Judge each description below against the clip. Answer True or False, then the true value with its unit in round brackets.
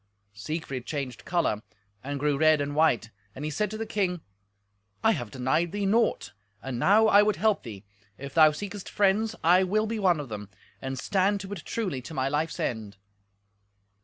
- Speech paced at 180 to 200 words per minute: True (190 wpm)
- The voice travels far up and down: True (7.3 semitones)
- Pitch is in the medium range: True (160 Hz)